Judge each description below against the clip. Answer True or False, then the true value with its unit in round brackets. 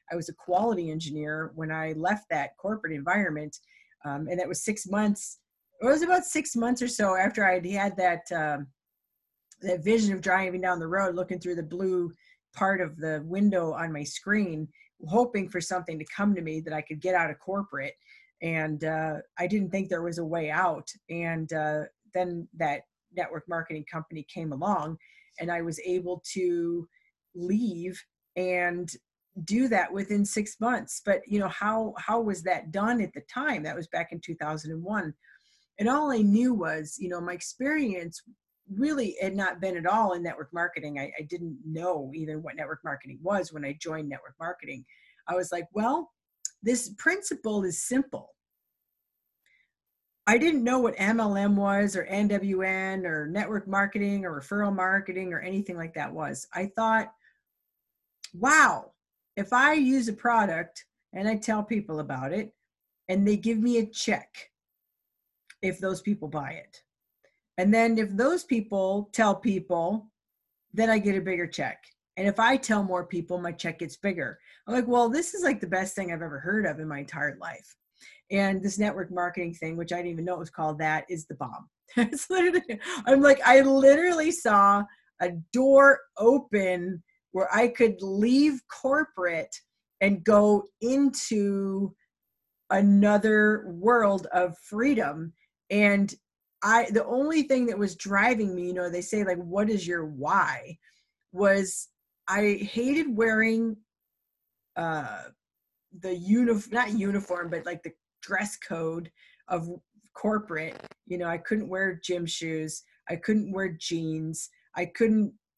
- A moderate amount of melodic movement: True (4.3 semitones)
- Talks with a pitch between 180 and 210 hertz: True (190 Hz)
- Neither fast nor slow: True (165 wpm)